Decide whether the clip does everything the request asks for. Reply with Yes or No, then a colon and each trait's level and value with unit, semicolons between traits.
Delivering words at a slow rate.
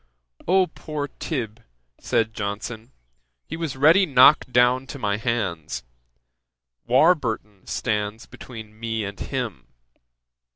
Yes: slow, 110 wpm